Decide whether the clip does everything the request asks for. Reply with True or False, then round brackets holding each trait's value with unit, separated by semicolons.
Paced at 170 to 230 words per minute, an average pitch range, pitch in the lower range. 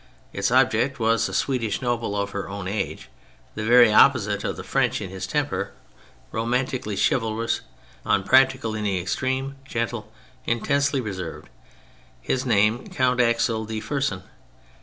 False (140 wpm; 3.8 semitones; 115 Hz)